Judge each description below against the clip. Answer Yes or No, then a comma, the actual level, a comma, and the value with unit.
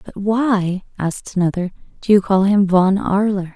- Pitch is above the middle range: Yes, high, 195 Hz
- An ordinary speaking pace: Yes, average, 170 wpm